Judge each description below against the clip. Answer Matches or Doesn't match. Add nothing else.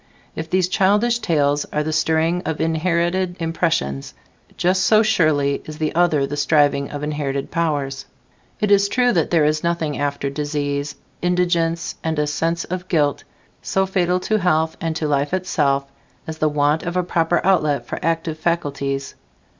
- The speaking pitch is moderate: Matches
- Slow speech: Doesn't match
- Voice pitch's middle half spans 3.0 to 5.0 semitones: Matches